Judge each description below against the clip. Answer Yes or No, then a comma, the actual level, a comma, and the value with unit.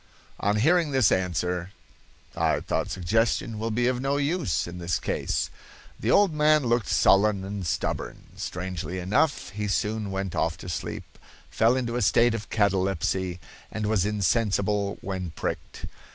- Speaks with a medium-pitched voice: No, low, 105 Hz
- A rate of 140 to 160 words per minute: Yes, average, 150 wpm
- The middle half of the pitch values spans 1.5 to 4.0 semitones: No, average, 4.4 semitones